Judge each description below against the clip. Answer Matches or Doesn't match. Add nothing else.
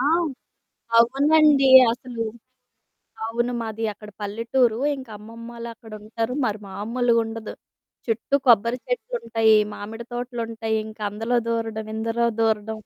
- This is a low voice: Doesn't match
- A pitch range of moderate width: Doesn't match